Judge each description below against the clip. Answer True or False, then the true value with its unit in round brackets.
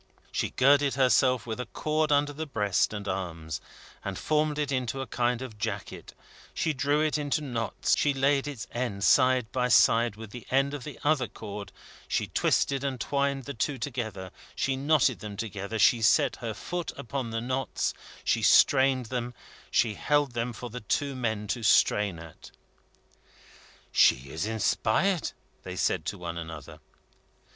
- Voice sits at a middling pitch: False (125 Hz)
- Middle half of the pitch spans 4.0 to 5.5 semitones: True (4.5 semitones)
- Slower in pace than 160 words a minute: False (170 wpm)